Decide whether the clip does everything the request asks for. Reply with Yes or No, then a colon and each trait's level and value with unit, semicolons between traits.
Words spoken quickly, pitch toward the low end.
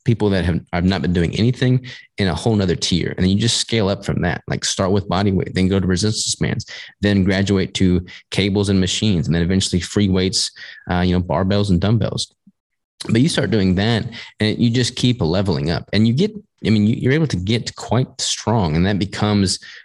Yes: fast, 220 wpm; low, 100 Hz